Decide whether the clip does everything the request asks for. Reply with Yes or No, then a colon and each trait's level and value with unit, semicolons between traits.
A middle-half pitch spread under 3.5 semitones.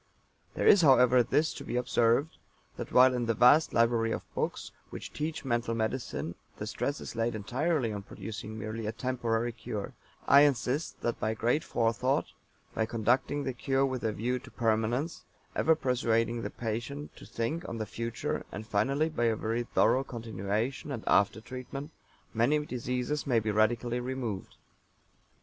Yes: average, 2.8 semitones